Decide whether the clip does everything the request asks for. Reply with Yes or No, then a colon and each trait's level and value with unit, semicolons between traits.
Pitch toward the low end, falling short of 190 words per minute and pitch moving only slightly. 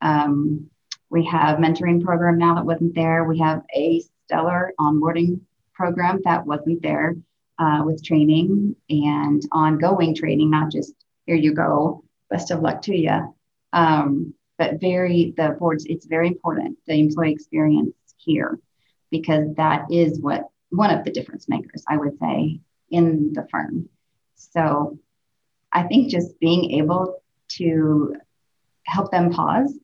No: medium, 165 Hz; average, 145 wpm; narrow, 2.1 semitones